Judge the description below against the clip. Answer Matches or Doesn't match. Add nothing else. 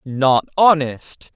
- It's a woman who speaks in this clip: Doesn't match